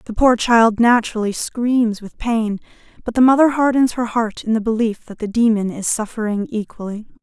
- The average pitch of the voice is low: No, high, 225 Hz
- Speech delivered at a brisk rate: No, average, 185 wpm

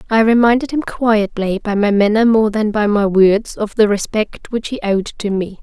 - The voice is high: Yes, high, 210 Hz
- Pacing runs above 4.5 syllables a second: Yes, 4.7 syllables/s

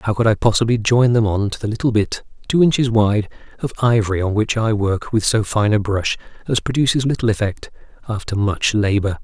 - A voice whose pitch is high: No, low, 110 Hz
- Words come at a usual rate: No, fast, 210 wpm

